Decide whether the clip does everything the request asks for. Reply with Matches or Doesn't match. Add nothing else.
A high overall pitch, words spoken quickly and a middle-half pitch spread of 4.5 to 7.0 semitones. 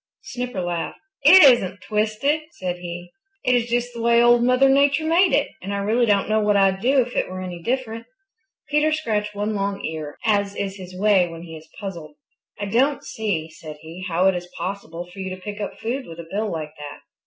Matches